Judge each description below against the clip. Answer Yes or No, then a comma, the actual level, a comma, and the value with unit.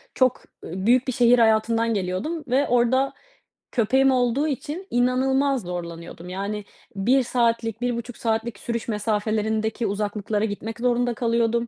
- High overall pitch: Yes, high, 235 Hz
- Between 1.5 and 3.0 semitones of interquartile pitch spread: Yes, average, 2.7 semitones